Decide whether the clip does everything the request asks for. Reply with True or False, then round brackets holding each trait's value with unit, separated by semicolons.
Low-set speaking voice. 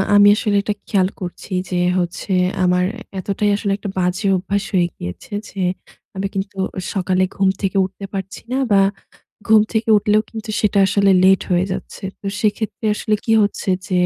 False (195 Hz)